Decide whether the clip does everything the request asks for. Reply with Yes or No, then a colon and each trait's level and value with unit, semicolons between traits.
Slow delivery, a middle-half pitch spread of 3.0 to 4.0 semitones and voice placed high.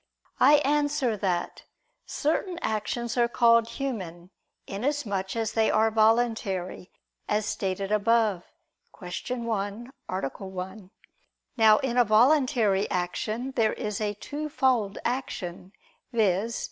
Yes: slow, 110 wpm; average, 3.7 semitones; high, 220 Hz